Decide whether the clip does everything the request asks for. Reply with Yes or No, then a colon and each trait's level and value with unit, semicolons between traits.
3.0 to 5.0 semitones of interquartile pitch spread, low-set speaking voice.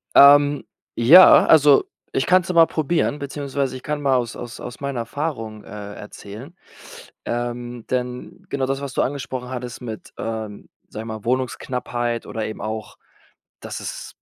Yes: average, 3.5 semitones; low, 125 Hz